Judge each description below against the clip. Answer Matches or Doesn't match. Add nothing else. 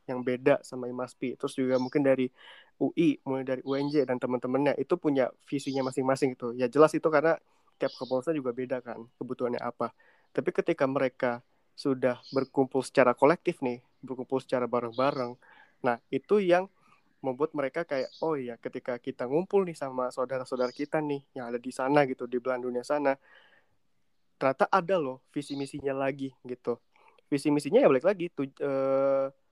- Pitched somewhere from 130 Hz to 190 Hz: Matches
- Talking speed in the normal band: Doesn't match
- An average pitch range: Doesn't match